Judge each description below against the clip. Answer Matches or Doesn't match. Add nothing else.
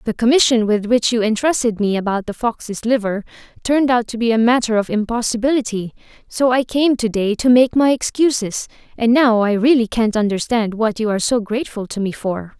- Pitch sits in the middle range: Doesn't match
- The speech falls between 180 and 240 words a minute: Matches